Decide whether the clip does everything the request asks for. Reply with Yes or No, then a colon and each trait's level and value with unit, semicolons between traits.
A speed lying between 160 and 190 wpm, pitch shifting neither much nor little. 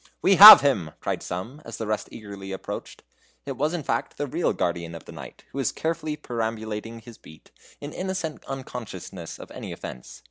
No: average, 185 wpm; wide, 7.3 semitones